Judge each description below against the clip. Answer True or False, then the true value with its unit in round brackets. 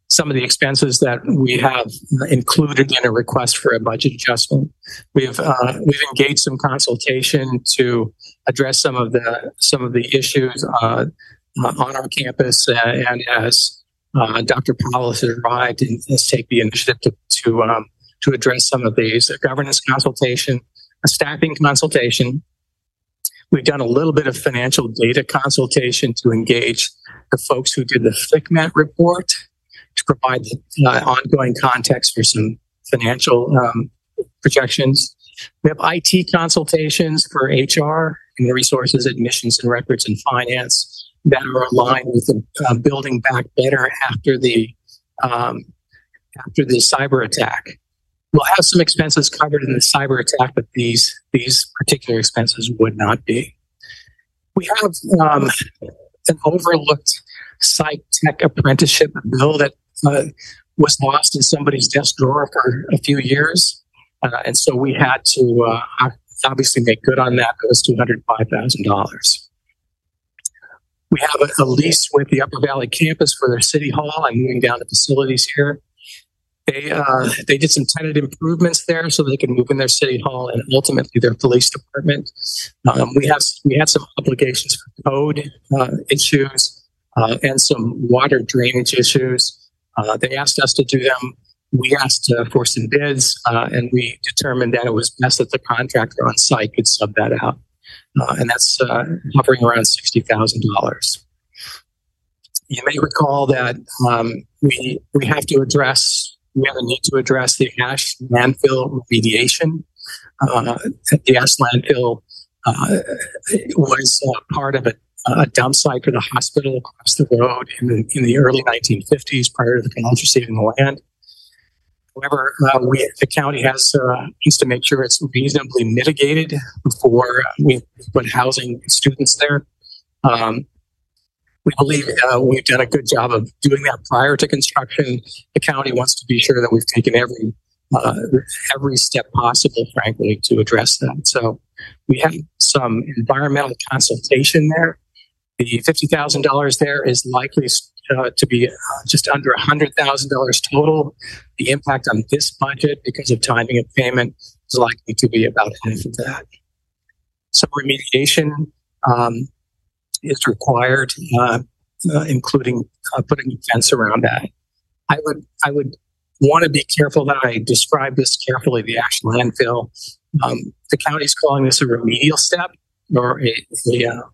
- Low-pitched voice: True (130 Hz)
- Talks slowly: False (160 wpm)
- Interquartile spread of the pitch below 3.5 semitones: True (3.1 semitones)